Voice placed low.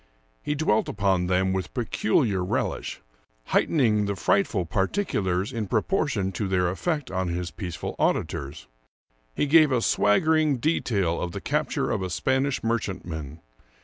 Yes: low, 100 Hz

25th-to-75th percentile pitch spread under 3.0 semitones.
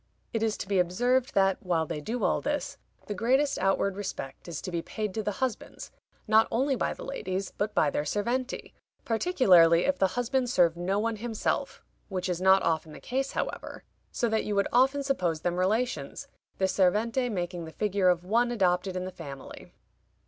No: average, 5.0 semitones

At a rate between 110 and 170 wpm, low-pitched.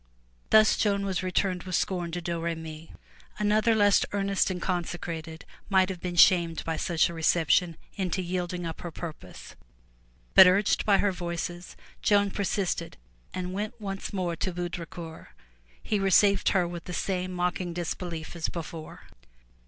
No: average, 150 wpm; medium, 180 Hz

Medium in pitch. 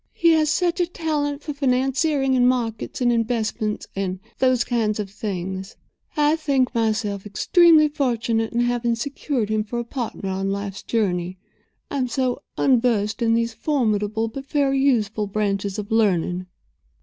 No: high, 230 Hz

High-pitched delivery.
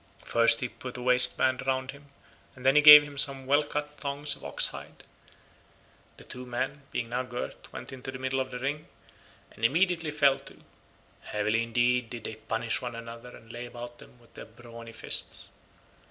No: low, 125 Hz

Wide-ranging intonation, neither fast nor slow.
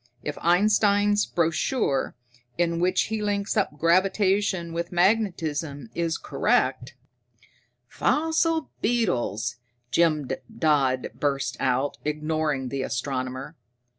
No: wide, 6.7 semitones; slow, 100 wpm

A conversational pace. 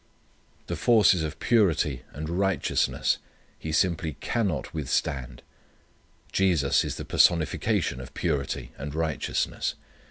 No: slow, 105 wpm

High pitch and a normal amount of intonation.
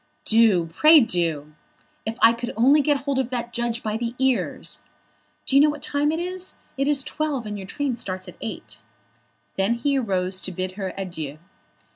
No: high, 235 Hz; wide, 6.6 semitones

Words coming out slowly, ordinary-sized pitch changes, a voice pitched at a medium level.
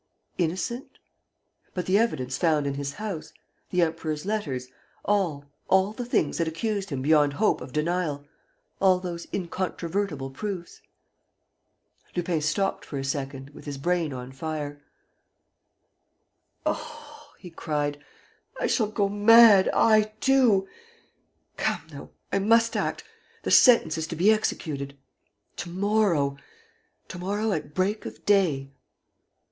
No: slow, 130 wpm; wide, 5.8 semitones; medium, 175 Hz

